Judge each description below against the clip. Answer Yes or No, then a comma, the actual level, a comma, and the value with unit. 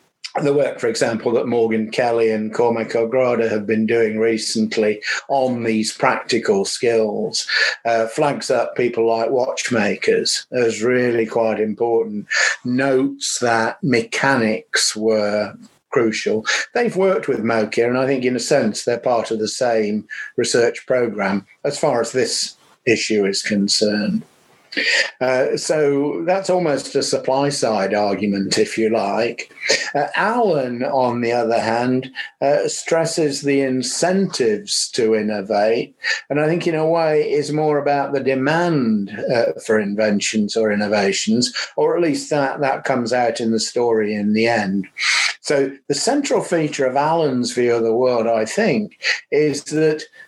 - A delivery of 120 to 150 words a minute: Yes, average, 145 wpm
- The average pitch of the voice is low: Yes, low, 120 Hz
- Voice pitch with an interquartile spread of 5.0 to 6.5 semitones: No, average, 4.6 semitones